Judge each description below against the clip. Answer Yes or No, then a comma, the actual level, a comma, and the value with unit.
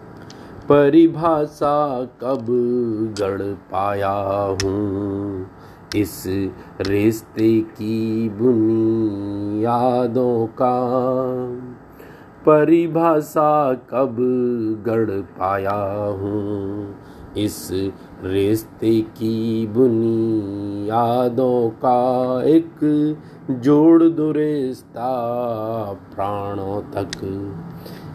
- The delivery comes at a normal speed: No, slow, 60 wpm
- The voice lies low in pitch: Yes, low, 115 Hz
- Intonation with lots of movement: No, average, 4.1 semitones